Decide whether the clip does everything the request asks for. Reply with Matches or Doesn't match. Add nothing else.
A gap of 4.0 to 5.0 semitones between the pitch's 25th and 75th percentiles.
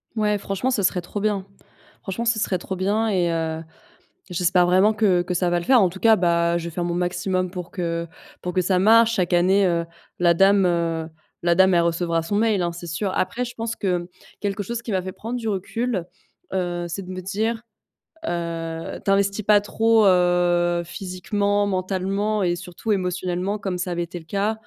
Doesn't match